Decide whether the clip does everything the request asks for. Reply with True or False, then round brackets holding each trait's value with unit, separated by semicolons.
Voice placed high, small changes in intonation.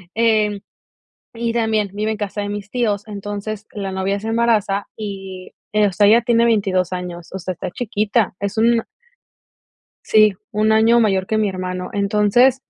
True (210 Hz; 2.1 semitones)